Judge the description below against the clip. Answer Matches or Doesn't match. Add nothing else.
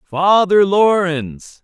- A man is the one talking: Matches